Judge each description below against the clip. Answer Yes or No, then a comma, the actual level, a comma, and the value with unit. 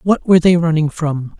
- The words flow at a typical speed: No, fast, 215 wpm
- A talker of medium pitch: Yes, medium, 165 Hz